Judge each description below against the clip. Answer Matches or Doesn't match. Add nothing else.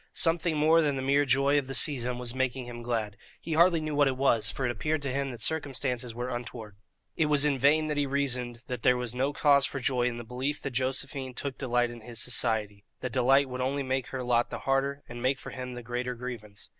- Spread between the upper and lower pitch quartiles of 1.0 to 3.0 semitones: Matches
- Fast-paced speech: Matches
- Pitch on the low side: Matches